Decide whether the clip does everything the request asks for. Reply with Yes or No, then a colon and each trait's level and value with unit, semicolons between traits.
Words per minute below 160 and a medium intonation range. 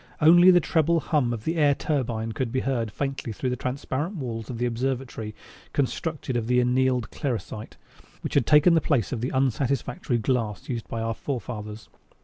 No: average, 180 wpm; average, 3.7 semitones